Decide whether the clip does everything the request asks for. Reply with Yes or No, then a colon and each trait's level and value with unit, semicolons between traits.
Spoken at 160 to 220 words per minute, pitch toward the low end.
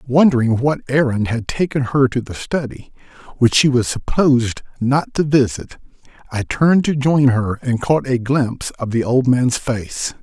Yes: average, 175 wpm; low, 130 Hz